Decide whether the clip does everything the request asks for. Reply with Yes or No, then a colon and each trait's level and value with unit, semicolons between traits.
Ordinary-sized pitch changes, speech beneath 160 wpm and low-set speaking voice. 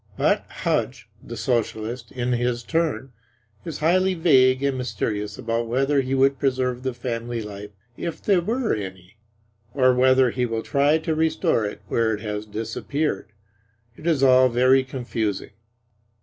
Yes: average, 3.4 semitones; average, 150 wpm; low, 130 Hz